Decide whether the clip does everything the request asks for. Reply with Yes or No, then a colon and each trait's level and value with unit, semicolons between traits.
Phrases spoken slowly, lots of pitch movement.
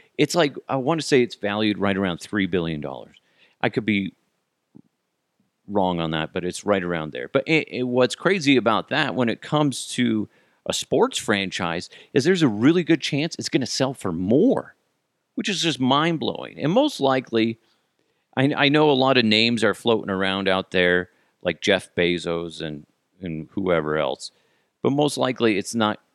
No: average, 190 wpm; wide, 6.5 semitones